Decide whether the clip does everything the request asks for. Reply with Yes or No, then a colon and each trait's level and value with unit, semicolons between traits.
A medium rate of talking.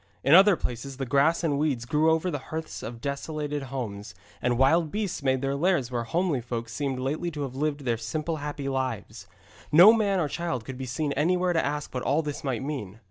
No: fast, 215 wpm